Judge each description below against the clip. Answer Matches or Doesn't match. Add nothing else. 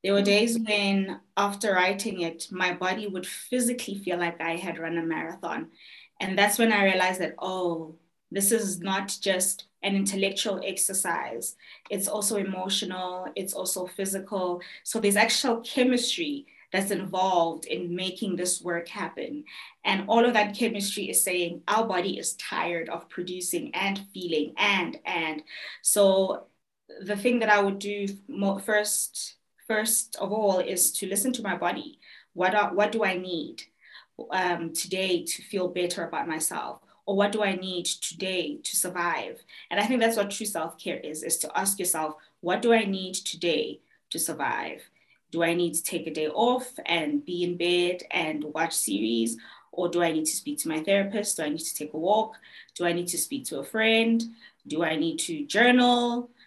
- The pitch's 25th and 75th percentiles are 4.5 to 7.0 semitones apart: Doesn't match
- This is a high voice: Matches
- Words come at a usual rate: Matches